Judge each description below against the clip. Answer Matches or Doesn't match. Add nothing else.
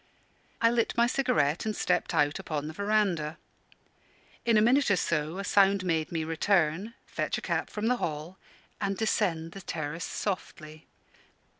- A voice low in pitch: Doesn't match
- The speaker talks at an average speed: Matches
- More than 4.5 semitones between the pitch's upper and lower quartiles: Matches